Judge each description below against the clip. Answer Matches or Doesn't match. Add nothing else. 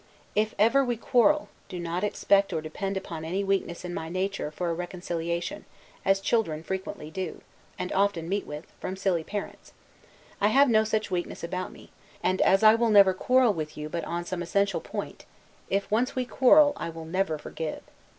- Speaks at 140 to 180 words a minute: Doesn't match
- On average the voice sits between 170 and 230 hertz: Matches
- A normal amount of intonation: Matches